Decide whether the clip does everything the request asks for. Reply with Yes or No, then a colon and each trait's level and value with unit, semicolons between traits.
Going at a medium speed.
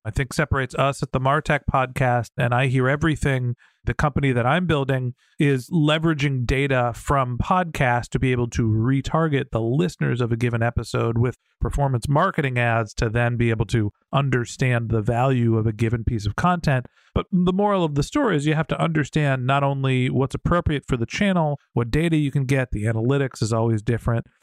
Yes: average, 195 wpm